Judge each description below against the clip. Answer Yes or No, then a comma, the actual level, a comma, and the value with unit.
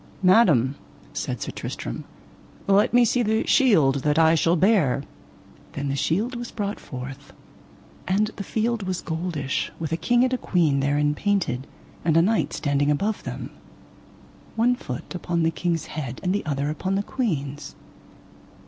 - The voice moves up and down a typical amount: No, wide, 6.4 semitones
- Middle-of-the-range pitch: Yes, medium, 170 Hz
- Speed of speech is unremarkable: Yes, average, 160 wpm